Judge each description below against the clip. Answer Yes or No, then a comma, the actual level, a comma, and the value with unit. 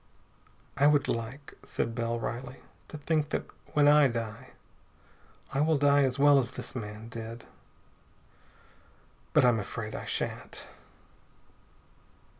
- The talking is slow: Yes, slow, 125 wpm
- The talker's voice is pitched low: Yes, low, 125 Hz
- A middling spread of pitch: Yes, average, 3.8 semitones